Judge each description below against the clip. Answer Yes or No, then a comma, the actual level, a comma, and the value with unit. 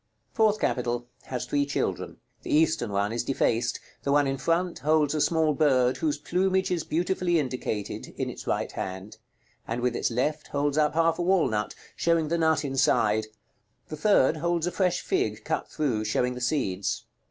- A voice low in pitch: No, medium, 145 Hz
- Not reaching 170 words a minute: No, average, 175 wpm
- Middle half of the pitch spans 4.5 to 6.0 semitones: Yes, average, 5.1 semitones